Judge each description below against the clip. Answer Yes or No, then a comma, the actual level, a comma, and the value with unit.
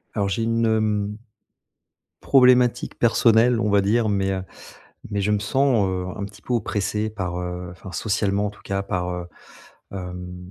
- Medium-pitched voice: No, low, 100 Hz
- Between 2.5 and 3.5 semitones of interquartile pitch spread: Yes, average, 3.1 semitones